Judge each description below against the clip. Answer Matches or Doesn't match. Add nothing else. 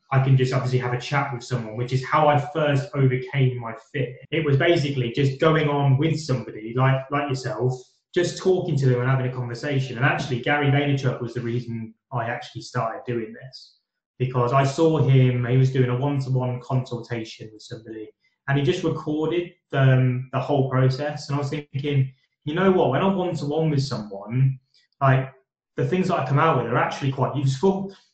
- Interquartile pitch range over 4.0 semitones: Doesn't match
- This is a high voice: Doesn't match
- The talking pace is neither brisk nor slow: Matches